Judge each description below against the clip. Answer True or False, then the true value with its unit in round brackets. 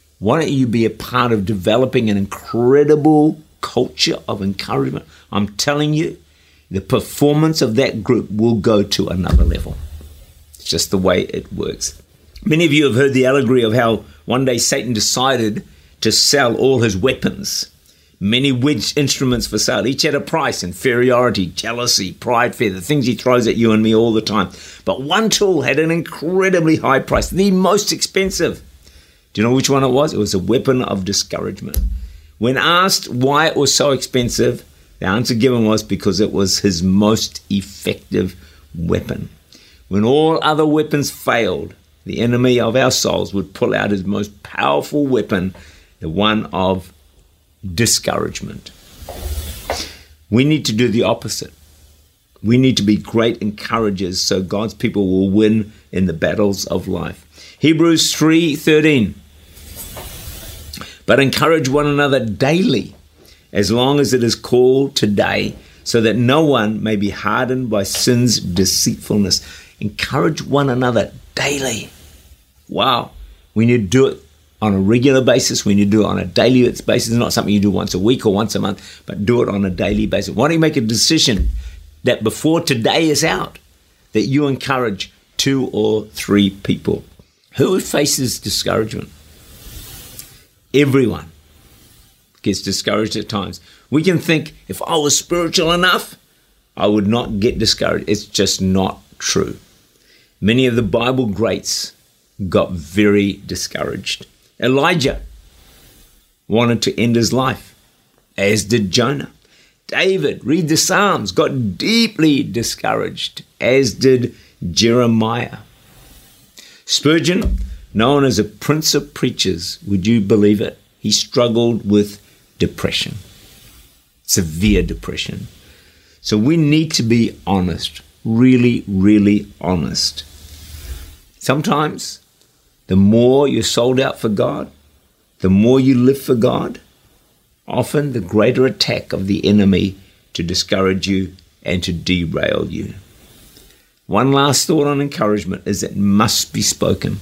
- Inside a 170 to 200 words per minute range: False (145 wpm)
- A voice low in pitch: True (110 Hz)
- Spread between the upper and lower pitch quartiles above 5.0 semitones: True (5.6 semitones)